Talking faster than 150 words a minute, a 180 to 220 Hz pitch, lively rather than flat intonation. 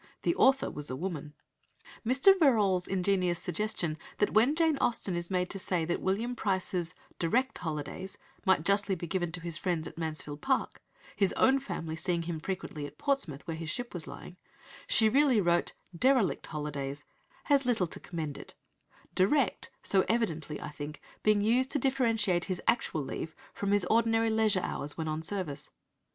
Yes: average, 170 wpm; medium, 185 Hz; wide, 5.8 semitones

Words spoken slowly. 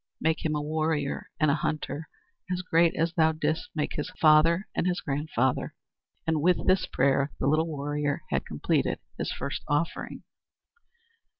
No: average, 155 wpm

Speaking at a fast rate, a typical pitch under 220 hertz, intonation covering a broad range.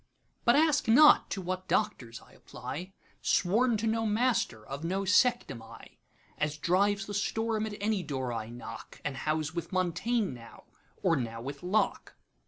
No: average, 155 wpm; medium, 185 Hz; wide, 7.7 semitones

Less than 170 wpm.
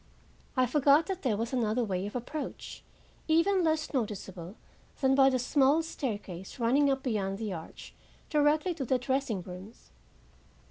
Yes: average, 150 wpm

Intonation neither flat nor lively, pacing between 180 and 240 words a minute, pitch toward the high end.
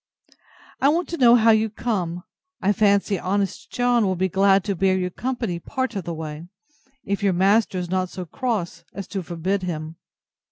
Yes: average, 3.6 semitones; average, 190 wpm; high, 195 Hz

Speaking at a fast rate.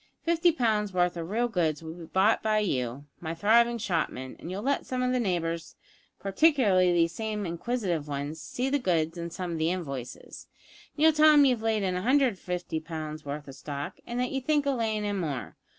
Yes: fast, 210 wpm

